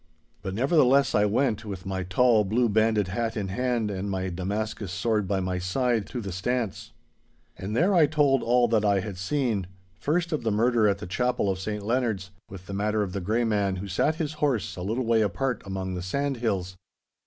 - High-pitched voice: No, low, 105 Hz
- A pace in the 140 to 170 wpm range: No, average, 200 wpm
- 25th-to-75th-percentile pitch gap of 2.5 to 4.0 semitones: No, average, 4.5 semitones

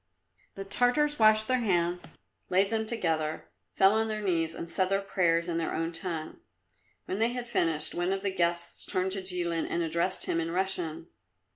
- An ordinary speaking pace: Yes, average, 185 wpm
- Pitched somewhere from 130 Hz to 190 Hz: Yes, medium, 185 Hz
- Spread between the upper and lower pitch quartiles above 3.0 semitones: Yes, average, 3.4 semitones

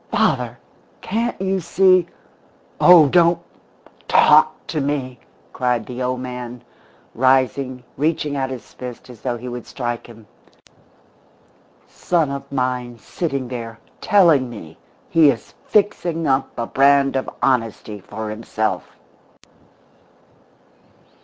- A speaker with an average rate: No, slow, 120 wpm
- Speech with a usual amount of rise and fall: Yes, average, 4.1 semitones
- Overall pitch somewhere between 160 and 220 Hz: No, low, 130 Hz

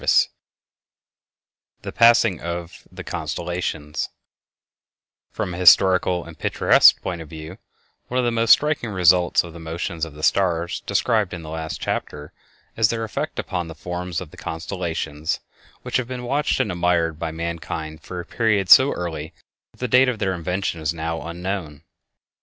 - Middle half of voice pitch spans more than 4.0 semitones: No, average, 3.5 semitones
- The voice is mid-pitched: No, very low, 90 Hz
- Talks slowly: No, average, 165 wpm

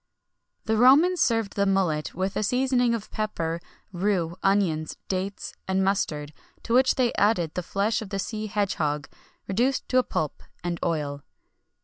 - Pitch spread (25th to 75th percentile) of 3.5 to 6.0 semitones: Yes, average, 5.0 semitones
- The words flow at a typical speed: Yes, average, 160 wpm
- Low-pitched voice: No, high, 195 Hz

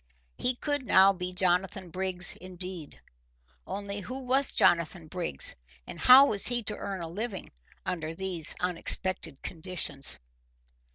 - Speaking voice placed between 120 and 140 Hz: No, medium, 185 Hz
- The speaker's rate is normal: No, slow, 130 wpm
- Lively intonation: No, average, 2.9 semitones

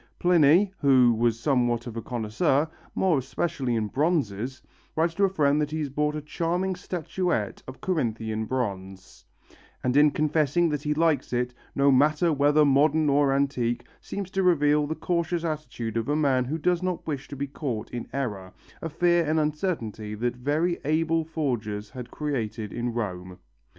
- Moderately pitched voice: Yes, medium, 145 Hz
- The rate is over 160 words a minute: Yes, average, 170 wpm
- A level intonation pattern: No, average, 4.9 semitones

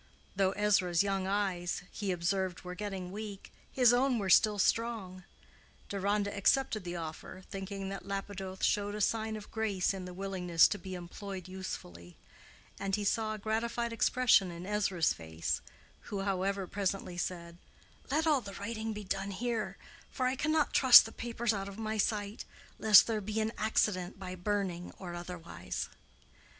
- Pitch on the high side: Yes, high, 195 Hz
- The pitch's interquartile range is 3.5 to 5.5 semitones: No, average, 2.8 semitones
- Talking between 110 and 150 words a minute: No, average, 160 wpm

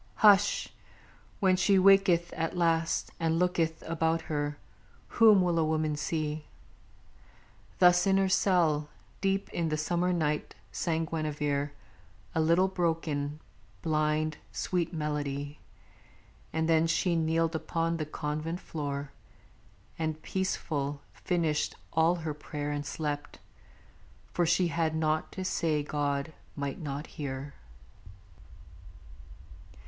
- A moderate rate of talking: No, slow, 115 wpm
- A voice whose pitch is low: No, medium, 160 Hz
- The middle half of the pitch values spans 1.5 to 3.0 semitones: Yes, narrow, 2.5 semitones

